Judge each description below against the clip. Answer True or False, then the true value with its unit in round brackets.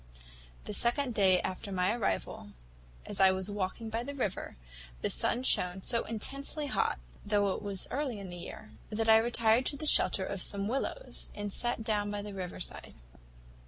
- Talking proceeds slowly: False (185 wpm)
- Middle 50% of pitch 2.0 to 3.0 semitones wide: False (3.7 semitones)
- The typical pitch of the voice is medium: False (210 Hz)